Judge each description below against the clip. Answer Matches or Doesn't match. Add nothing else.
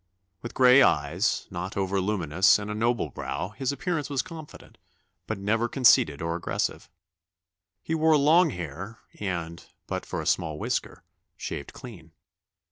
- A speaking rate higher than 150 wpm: Doesn't match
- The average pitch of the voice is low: Matches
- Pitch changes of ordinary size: Doesn't match